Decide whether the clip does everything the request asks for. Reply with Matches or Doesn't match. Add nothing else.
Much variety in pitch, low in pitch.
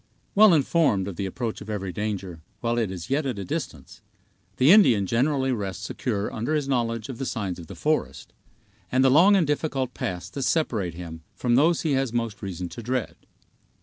Matches